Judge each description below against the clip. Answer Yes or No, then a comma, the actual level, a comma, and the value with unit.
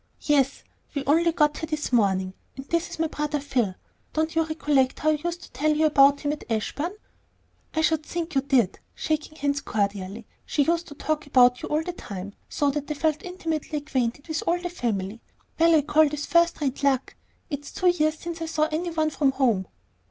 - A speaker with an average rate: No, fast, 210 wpm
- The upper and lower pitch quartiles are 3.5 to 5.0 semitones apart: No, average, 3.1 semitones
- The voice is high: Yes, very high, 295 Hz